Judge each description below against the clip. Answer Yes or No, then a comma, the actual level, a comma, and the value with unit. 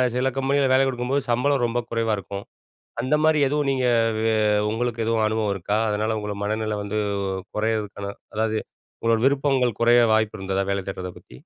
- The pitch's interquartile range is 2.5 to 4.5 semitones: Yes, average, 3.4 semitones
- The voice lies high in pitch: No, low, 115 Hz